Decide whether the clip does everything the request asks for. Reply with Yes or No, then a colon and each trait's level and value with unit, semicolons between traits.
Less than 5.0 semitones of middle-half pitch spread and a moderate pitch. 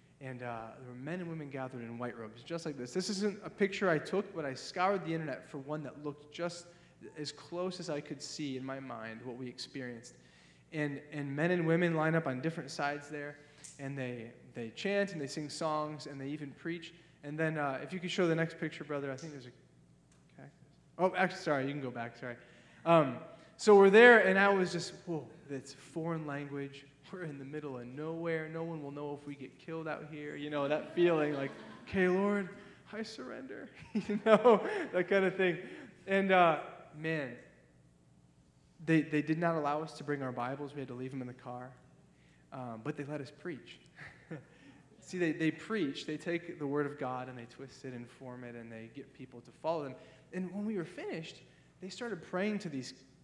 Yes: average, 4.3 semitones; medium, 150 Hz